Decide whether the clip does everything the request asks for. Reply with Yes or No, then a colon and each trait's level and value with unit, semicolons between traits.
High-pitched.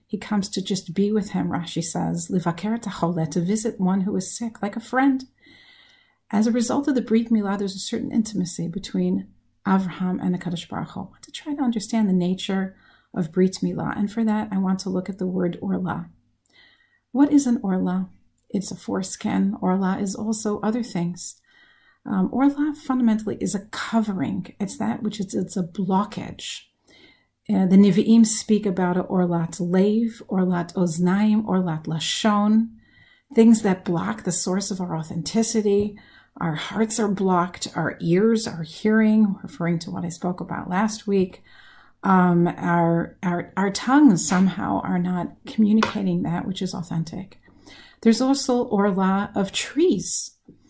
Yes: high, 195 Hz